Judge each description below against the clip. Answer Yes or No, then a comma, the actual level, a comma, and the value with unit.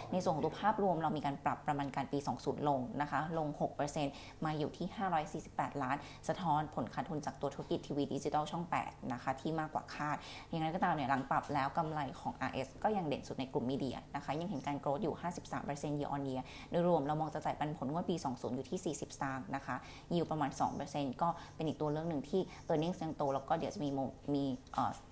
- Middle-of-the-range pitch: Yes, medium, 150 Hz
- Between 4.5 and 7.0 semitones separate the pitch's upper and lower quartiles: No, narrow, 2.4 semitones